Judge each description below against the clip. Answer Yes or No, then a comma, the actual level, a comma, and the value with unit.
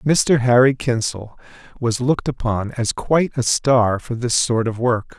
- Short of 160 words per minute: No, average, 175 wpm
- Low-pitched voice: Yes, low, 120 Hz